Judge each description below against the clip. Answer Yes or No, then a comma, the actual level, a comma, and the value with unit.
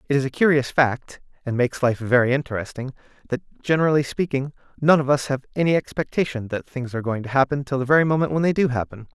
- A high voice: No, low, 135 Hz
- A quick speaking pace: Yes, fast, 215 wpm